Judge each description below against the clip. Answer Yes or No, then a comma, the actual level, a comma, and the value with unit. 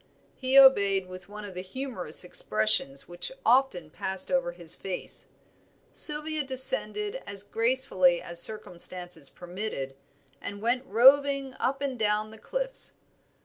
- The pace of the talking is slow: Yes, slow, 130 wpm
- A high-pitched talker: Yes, high, 210 Hz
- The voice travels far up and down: Yes, wide, 7.0 semitones